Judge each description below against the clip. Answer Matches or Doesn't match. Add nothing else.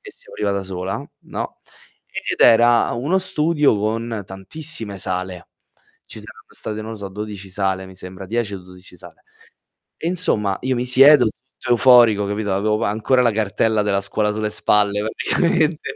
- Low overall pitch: Matches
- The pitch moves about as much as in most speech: Matches